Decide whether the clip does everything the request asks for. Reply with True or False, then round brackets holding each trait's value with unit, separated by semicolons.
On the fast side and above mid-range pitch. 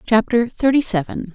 False (135 wpm; 225 Hz)